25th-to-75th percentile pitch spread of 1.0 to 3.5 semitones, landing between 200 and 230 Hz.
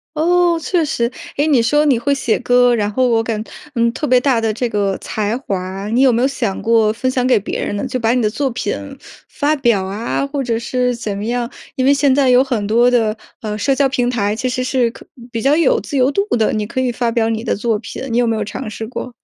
No: average, 3.0 semitones; high, 240 Hz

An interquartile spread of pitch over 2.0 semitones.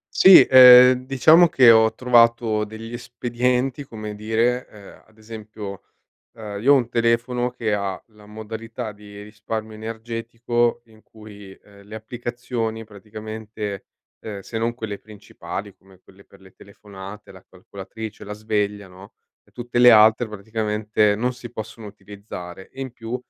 Yes: narrow, 2.4 semitones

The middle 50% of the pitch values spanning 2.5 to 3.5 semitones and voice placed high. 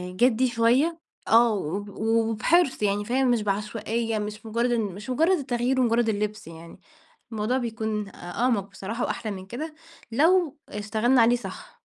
Yes: average, 2.9 semitones; high, 225 Hz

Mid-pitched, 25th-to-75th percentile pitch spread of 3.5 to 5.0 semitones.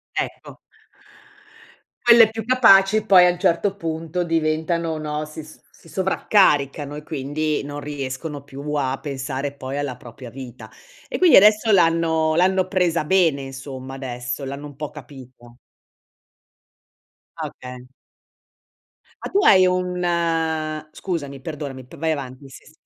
Yes: medium, 155 Hz; average, 4.4 semitones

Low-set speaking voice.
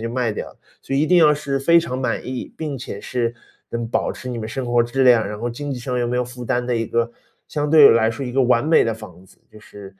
Yes: low, 125 Hz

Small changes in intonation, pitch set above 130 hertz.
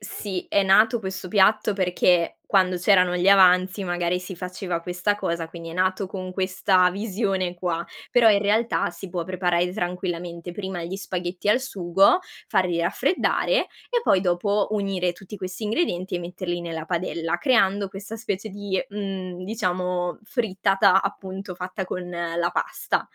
Yes: narrow, 2.2 semitones; medium, 185 Hz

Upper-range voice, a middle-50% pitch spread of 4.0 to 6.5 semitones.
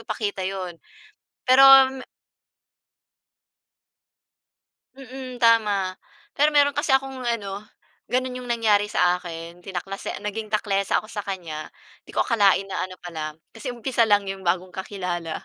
Yes: high, 205 Hz; average, 4.3 semitones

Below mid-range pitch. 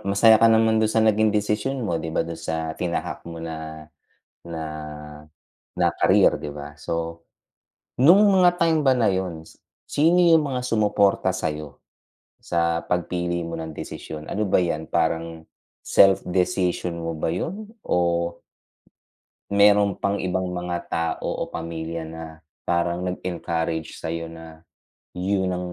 Yes: very low, 90 Hz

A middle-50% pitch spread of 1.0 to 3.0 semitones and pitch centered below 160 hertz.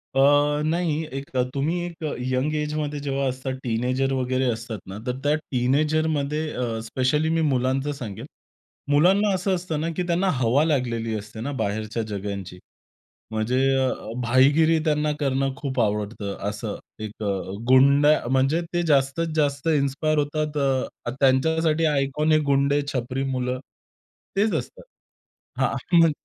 No: average, 3.6 semitones; low, 135 Hz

